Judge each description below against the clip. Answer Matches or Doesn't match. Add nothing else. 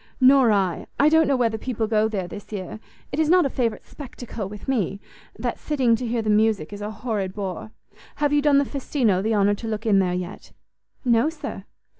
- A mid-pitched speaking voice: Doesn't match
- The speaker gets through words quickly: Matches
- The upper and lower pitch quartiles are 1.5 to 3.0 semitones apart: Doesn't match